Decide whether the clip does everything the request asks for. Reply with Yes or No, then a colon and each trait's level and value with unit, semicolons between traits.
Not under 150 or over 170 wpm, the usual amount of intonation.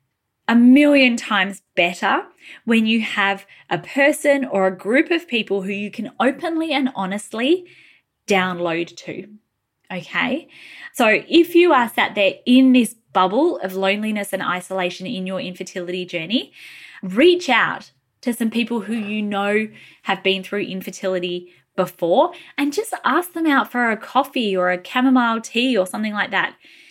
No: average, 155 wpm; wide, 6.2 semitones